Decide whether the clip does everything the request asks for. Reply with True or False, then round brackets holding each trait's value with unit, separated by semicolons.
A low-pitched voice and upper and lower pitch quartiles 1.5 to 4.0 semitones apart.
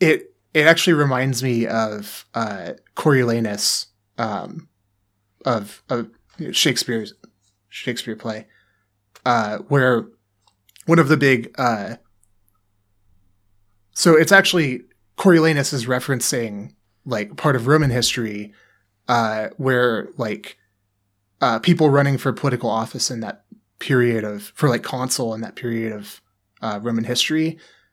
False (115 Hz; 4.8 semitones)